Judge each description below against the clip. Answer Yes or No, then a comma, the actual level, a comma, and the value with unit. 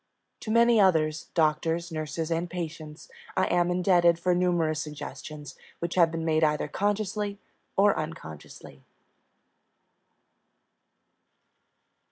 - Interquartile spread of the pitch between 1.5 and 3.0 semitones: Yes, average, 2.7 semitones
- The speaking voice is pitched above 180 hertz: No, medium, 165 Hz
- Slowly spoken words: Yes, slow, 105 wpm